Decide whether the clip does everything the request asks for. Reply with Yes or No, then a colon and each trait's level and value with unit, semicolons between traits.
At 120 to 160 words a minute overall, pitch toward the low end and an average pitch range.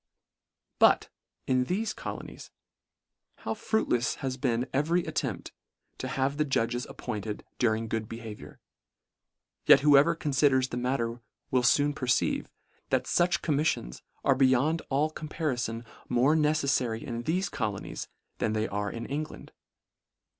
Yes: slow, 135 wpm; low, 130 Hz; average, 4.4 semitones